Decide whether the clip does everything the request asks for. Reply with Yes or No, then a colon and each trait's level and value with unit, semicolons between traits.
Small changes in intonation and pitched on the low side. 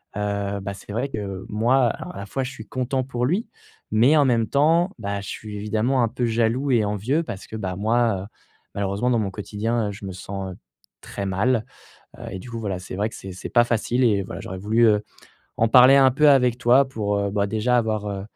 No: average, 3.7 semitones; low, 110 Hz